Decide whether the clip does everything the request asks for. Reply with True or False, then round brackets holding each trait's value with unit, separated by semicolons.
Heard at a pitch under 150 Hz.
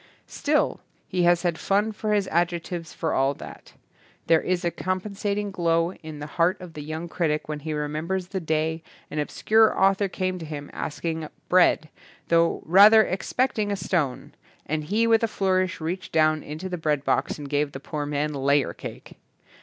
False (170 Hz)